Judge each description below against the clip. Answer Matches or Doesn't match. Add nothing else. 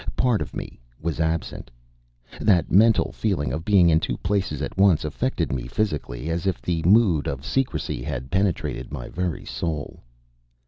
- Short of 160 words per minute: Doesn't match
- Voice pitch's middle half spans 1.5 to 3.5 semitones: Doesn't match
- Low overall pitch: Matches